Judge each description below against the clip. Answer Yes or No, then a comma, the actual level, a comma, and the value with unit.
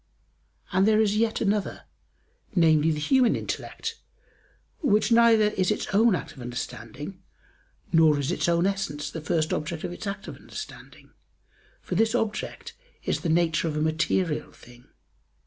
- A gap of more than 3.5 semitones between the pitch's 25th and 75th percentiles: Yes, average, 5.3 semitones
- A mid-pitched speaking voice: Yes, medium, 175 Hz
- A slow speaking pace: No, average, 155 wpm